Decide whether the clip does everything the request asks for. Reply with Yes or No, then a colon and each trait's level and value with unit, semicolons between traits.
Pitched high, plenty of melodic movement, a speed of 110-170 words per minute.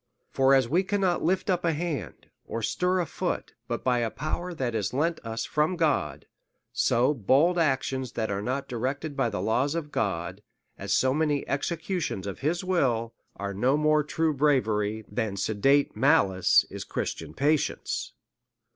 No: low, 135 Hz; wide, 5.9 semitones; average, 165 wpm